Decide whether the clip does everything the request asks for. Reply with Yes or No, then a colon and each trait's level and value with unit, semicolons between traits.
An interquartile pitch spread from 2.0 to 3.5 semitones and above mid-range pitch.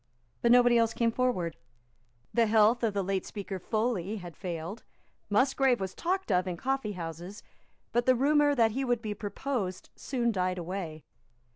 No: average, 4.8 semitones; high, 215 Hz